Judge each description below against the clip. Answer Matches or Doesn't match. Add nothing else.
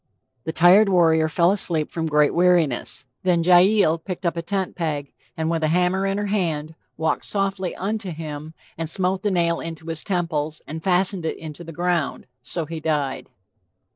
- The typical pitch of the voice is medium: Matches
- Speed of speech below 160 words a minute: Doesn't match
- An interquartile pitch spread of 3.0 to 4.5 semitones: Doesn't match